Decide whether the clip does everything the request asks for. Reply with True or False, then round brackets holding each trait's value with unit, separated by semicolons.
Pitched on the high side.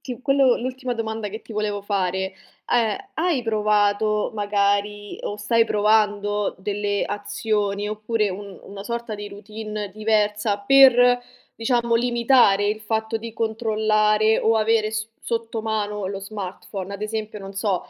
True (215 Hz)